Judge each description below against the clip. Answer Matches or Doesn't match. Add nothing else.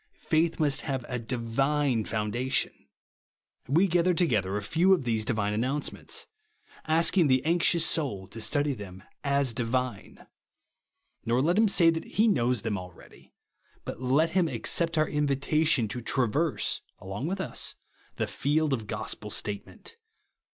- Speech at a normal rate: Matches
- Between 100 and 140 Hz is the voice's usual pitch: Matches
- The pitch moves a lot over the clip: Matches